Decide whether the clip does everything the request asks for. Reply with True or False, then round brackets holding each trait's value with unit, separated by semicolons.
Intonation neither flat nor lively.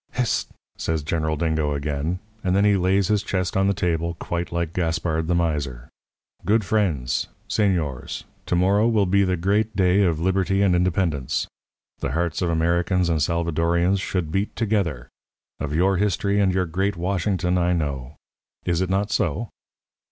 True (3.2 semitones)